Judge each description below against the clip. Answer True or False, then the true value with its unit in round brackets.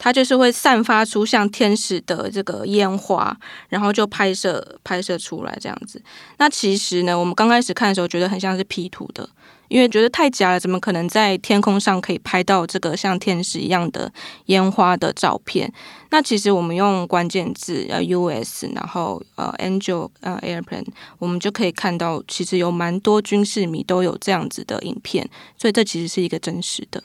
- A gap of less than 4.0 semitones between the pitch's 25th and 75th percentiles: True (2.8 semitones)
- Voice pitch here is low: False (190 Hz)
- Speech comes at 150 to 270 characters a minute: False (315 characters per minute)